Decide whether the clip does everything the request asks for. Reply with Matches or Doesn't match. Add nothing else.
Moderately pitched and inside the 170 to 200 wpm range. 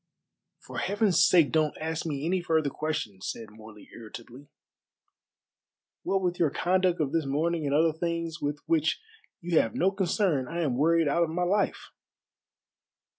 Doesn't match